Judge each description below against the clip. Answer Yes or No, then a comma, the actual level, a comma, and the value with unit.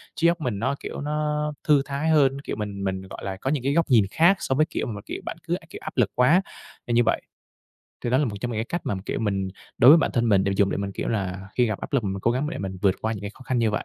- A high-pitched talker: No, low, 120 Hz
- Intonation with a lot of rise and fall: Yes, wide, 6.7 semitones